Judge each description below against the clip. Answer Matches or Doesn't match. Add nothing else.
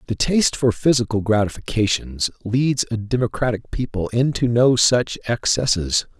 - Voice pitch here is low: Matches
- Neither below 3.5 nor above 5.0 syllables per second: Matches